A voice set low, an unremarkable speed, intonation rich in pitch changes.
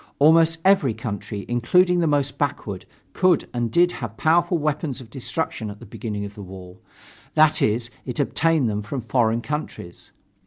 Yes: low, 125 Hz; average, 165 wpm; wide, 6.6 semitones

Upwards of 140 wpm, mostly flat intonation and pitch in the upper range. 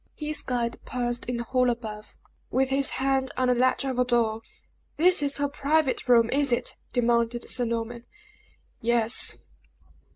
Yes: average, 160 wpm; narrow, 2.2 semitones; very high, 250 Hz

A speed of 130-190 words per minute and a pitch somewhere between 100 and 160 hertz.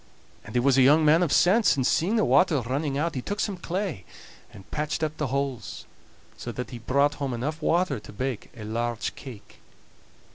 No: fast, 205 wpm; medium, 140 Hz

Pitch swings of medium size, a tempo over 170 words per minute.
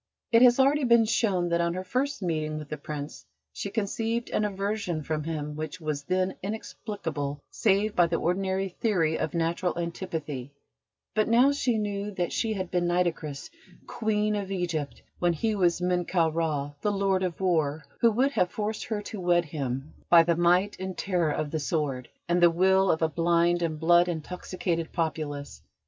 Yes: average, 4.1 semitones; average, 180 wpm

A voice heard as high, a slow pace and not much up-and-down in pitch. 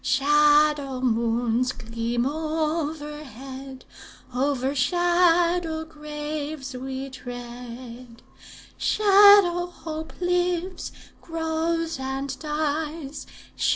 No: very high, 295 Hz; slow, 65 wpm; average, 3.8 semitones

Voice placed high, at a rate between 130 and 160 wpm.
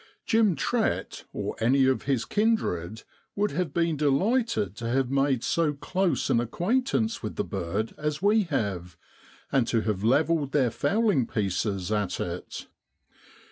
No: low, 135 Hz; average, 145 wpm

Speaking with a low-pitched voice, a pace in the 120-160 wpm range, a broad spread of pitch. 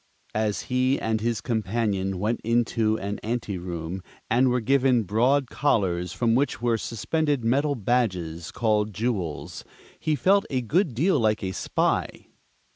No: low, 115 Hz; average, 140 wpm; average, 3.8 semitones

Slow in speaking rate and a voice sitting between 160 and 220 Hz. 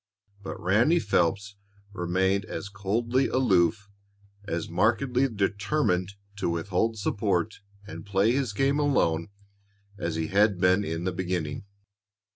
No: slow, 120 wpm; low, 100 Hz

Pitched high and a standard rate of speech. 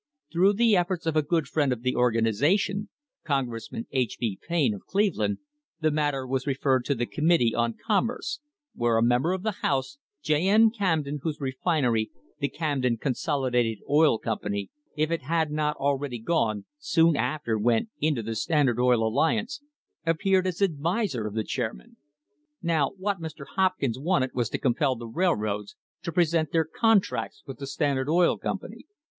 No: medium, 145 Hz; average, 170 wpm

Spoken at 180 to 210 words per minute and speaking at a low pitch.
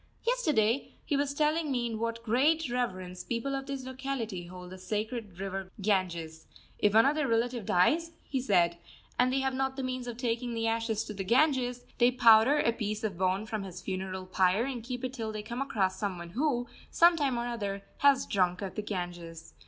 No: fast, 205 wpm; high, 230 Hz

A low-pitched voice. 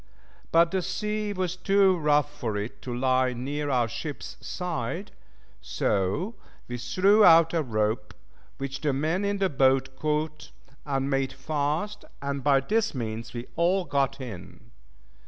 No: medium, 145 Hz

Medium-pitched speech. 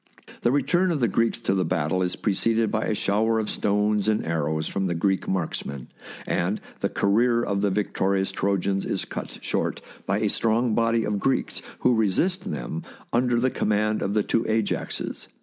No: low, 105 Hz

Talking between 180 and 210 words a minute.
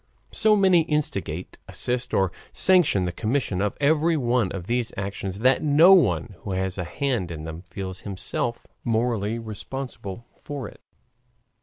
No: average, 150 wpm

